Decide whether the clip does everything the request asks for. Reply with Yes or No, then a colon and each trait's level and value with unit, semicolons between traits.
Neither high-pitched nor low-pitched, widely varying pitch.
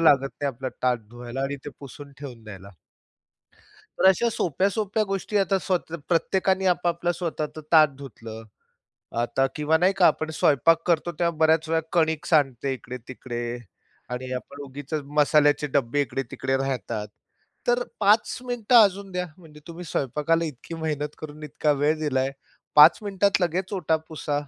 No: medium, 155 Hz; average, 4.6 semitones